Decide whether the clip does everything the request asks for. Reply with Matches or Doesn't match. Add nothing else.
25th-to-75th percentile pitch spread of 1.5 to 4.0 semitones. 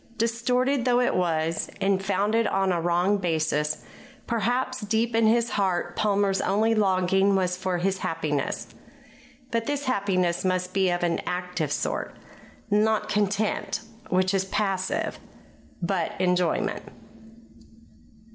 Matches